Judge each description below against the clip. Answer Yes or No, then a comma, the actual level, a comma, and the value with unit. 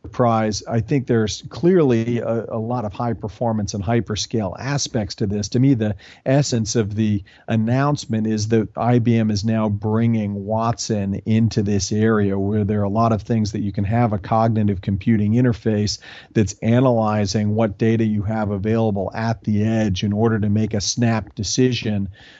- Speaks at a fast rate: No, average, 170 wpm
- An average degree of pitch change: No, narrow, 1.7 semitones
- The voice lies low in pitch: Yes, low, 110 Hz